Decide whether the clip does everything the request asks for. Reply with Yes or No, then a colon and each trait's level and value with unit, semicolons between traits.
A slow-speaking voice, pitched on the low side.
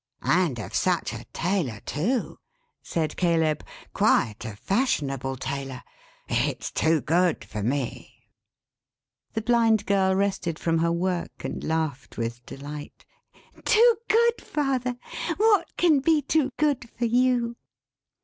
No: slow, 125 wpm; medium, 180 Hz